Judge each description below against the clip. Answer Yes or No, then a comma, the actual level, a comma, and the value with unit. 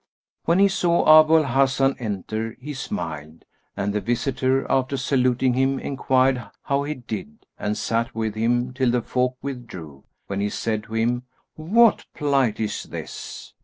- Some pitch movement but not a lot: Yes, average, 3.5 semitones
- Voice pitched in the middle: No, low, 125 Hz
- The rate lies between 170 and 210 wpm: No, average, 160 wpm